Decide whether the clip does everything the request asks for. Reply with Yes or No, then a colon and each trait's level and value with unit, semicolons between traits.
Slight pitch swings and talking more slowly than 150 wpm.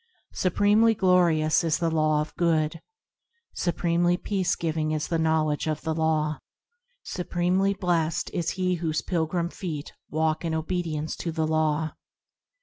Yes: narrow, 2.1 semitones; average, 140 wpm